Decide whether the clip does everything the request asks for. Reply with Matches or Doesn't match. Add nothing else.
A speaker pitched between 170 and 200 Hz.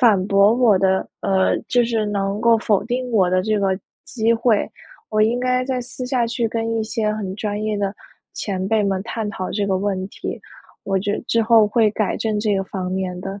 Doesn't match